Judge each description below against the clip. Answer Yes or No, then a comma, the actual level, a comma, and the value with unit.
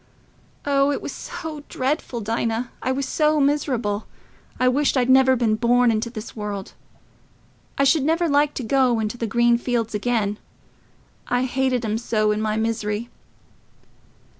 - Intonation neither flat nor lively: Yes, average, 3.6 semitones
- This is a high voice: Yes, high, 245 Hz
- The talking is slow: No, average, 150 wpm